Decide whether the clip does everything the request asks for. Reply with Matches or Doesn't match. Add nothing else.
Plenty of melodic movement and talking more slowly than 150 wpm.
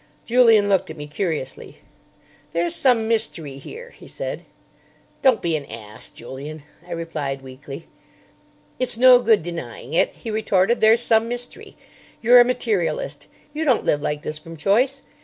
Doesn't match